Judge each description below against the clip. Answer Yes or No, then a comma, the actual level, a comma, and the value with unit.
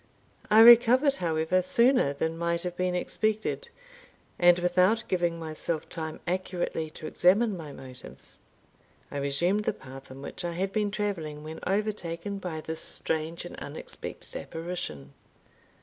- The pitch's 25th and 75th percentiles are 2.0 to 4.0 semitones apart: No, average, 4.4 semitones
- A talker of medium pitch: Yes, medium, 175 Hz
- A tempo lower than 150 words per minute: Yes, average, 140 wpm